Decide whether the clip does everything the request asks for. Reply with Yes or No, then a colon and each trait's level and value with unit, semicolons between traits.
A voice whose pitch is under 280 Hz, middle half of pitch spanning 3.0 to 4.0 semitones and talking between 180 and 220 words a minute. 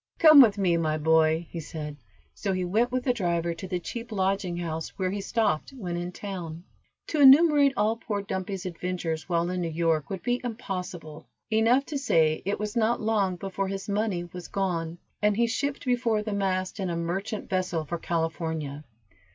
No: medium, 185 Hz; average, 4.5 semitones; average, 190 wpm